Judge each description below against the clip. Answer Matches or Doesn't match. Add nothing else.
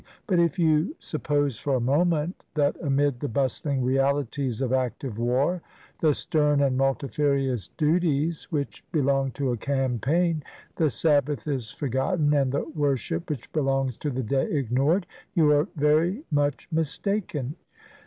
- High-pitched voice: Doesn't match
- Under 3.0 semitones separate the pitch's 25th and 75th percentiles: Matches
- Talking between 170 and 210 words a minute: Doesn't match